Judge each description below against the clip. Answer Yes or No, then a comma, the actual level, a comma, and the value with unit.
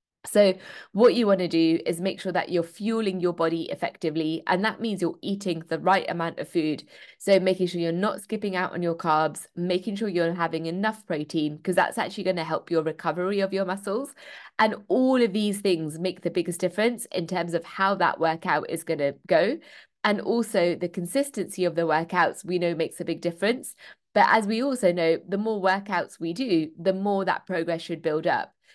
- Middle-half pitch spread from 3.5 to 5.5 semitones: No, average, 2.9 semitones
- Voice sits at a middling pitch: Yes, medium, 180 Hz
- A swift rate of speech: Yes, fast, 210 wpm